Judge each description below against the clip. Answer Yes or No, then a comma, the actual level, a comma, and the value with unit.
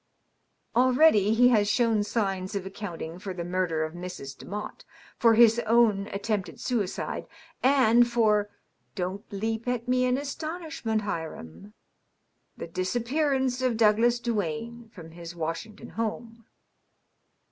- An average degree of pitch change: Yes, average, 4.5 semitones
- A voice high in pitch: Yes, high, 215 Hz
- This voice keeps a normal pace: No, slow, 130 wpm